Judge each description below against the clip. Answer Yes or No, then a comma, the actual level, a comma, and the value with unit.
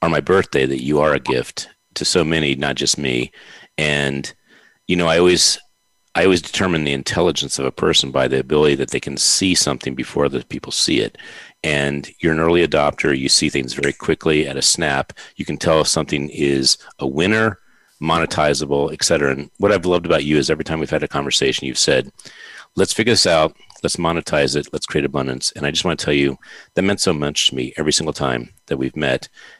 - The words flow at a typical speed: No, fast, 215 wpm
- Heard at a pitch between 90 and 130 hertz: No, very low, 75 Hz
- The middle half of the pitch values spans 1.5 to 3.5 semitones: Yes, average, 2.8 semitones